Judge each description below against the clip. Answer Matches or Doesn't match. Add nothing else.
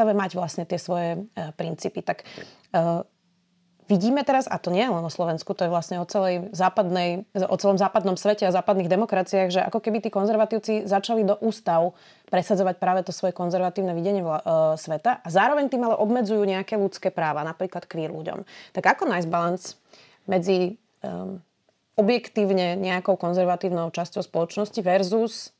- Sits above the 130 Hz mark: Matches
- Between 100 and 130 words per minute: Doesn't match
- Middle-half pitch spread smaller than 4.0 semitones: Matches